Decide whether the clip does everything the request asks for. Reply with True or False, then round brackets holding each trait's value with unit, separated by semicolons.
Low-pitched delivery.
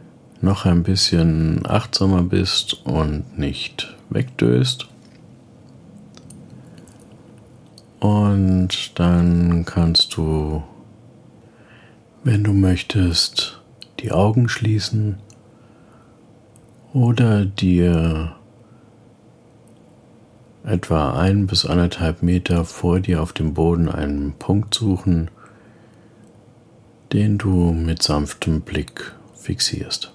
True (95 Hz)